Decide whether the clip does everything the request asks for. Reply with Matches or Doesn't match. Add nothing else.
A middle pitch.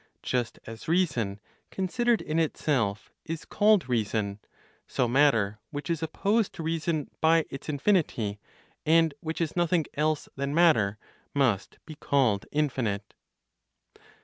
Matches